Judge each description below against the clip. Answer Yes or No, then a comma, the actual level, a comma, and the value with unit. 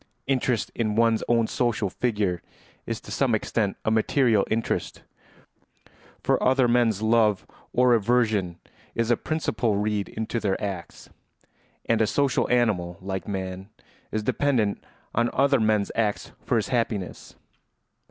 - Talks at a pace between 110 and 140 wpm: Yes, slow, 135 wpm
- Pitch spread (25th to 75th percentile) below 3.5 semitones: Yes, average, 2.8 semitones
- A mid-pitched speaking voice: No, low, 110 Hz